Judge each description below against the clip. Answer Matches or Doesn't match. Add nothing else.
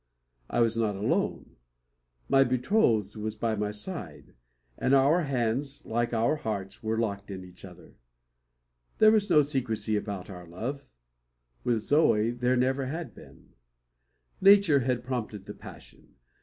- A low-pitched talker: Matches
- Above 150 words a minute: Doesn't match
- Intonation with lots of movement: Doesn't match